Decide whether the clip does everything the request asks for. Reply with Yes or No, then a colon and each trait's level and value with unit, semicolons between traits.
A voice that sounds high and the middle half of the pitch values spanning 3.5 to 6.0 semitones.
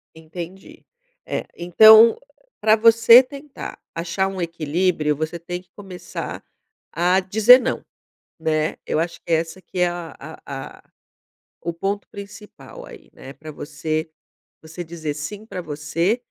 No: medium, 175 Hz; average, 4.2 semitones